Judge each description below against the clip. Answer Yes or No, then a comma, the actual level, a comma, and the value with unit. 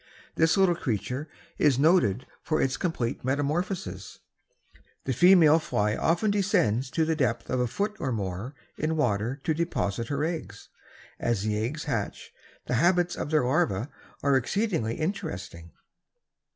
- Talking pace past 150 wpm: No, average, 145 wpm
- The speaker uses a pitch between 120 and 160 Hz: Yes, medium, 140 Hz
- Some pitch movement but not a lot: No, wide, 6.4 semitones